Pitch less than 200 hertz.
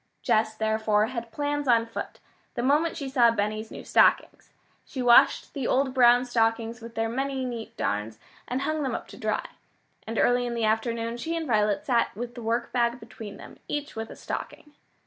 No: high, 235 Hz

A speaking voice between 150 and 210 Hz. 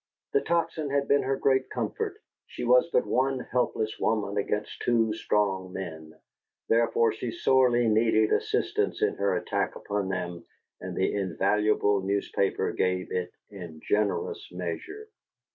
No: low, 105 Hz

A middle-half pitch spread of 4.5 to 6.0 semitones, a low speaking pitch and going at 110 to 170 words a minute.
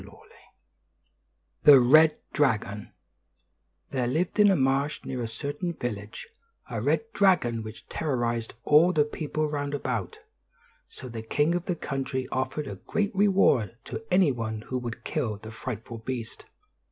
Yes: average, 4.9 semitones; low, 130 Hz; average, 150 wpm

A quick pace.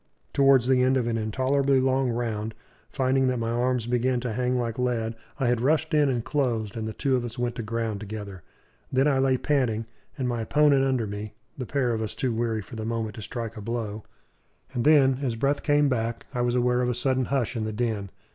Yes: fast, 230 wpm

